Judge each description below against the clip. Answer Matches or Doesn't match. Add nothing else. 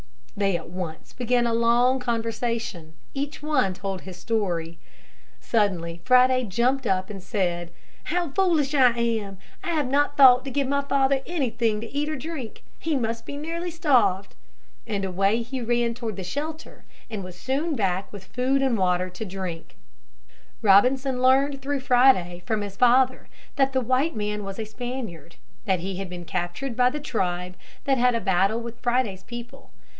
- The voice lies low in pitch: Doesn't match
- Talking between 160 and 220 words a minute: Matches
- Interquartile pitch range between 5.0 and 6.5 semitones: Matches